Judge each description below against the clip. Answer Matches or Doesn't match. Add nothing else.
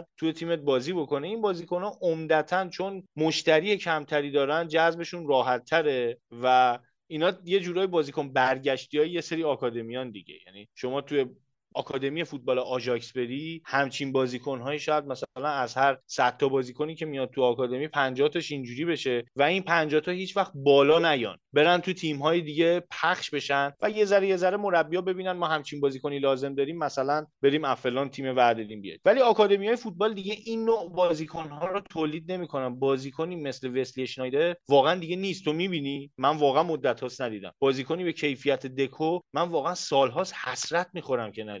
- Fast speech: Matches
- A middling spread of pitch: Matches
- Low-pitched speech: Doesn't match